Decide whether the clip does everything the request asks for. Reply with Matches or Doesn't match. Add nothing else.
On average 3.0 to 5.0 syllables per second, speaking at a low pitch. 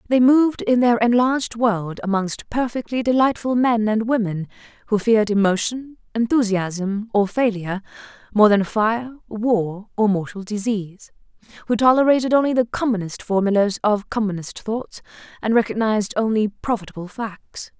Doesn't match